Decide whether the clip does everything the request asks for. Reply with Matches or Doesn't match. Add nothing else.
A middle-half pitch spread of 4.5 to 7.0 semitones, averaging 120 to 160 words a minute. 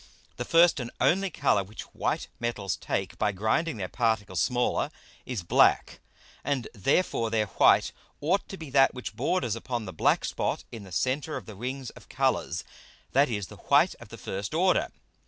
Doesn't match